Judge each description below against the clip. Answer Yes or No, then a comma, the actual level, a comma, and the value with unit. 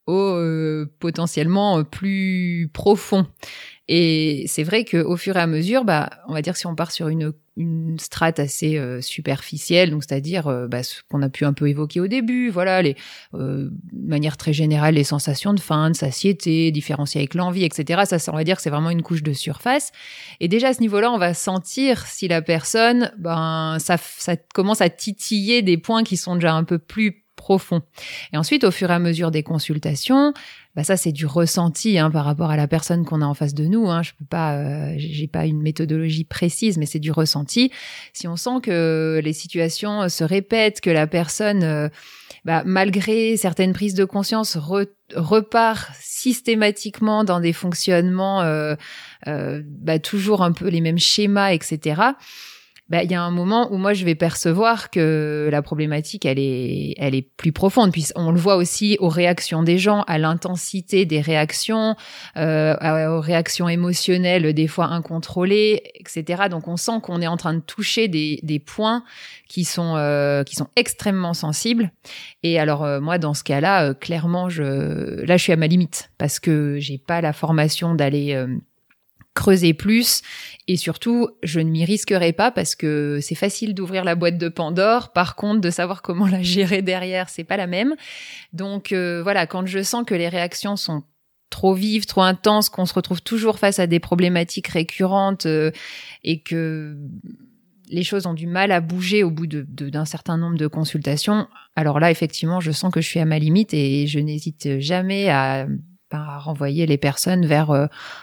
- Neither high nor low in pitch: Yes, medium, 170 Hz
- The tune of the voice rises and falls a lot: No, average, 3.9 semitones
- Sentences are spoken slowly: No, average, 195 wpm